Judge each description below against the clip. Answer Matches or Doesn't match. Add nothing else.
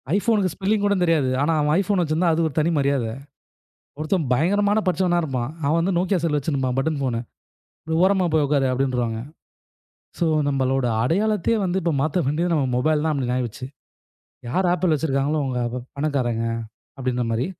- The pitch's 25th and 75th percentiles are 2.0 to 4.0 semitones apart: Doesn't match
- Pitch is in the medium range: Matches